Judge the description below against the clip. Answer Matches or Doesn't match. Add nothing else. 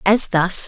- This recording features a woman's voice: Matches